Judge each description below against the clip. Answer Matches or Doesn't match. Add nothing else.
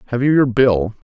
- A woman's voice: Doesn't match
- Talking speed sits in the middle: Doesn't match